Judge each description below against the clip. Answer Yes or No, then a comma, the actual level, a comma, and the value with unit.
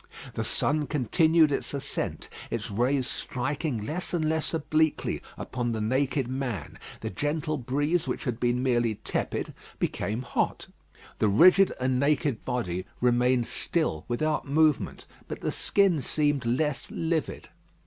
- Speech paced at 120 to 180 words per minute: Yes, average, 140 wpm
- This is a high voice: No, low, 135 Hz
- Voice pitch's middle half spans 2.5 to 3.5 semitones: No, average, 4.2 semitones